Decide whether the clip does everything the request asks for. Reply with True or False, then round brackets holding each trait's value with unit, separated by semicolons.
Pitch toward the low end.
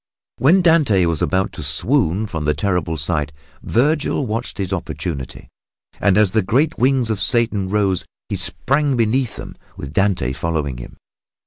True (100 Hz)